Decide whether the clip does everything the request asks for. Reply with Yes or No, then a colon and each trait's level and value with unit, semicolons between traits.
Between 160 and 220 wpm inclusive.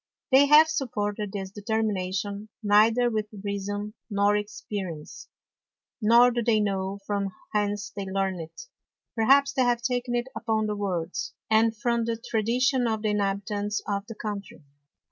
No: average, 145 wpm